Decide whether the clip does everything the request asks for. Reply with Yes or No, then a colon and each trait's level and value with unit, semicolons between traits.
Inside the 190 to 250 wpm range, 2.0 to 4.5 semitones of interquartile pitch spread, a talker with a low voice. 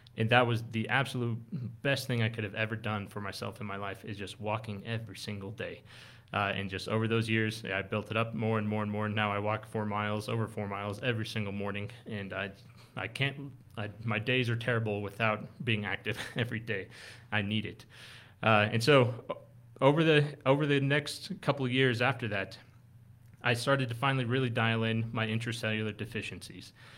Yes: average, 200 wpm; narrow, 2.6 semitones; low, 115 Hz